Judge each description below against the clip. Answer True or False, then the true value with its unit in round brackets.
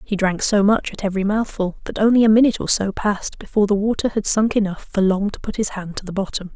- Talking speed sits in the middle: False (265 wpm)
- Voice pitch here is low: False (205 Hz)